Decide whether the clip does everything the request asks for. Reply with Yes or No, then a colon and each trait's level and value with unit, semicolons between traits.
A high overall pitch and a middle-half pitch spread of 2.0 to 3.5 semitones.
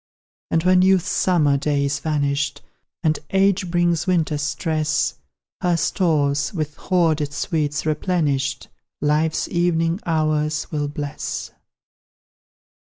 No: medium, 155 Hz; average, 2.9 semitones